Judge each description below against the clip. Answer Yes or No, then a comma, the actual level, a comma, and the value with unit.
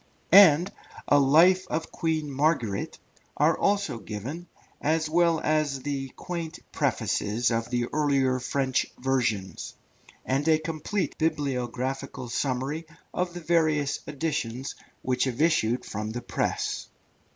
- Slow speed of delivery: Yes, slow, 120 wpm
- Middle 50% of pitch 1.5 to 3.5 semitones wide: No, average, 4.1 semitones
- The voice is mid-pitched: Yes, medium, 145 Hz